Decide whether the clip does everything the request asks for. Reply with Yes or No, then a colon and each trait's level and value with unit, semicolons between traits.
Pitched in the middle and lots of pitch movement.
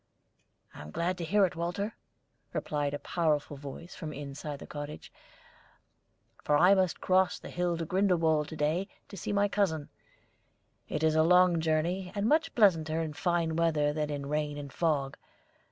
No: medium, 160 Hz; average, 3.5 semitones